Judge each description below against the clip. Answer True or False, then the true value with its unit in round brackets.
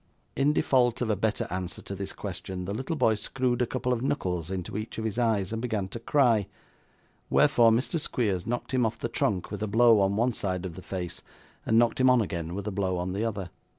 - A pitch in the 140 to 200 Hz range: False (110 Hz)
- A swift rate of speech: True (235 wpm)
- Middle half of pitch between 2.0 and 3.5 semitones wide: False (4.3 semitones)